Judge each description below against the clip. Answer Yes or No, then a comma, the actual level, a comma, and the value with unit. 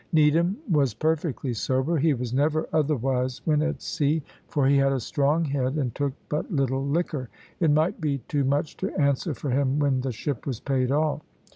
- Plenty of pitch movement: No, average, 2.7 semitones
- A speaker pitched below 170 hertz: Yes, medium, 140 Hz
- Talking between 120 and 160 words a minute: No, average, 190 wpm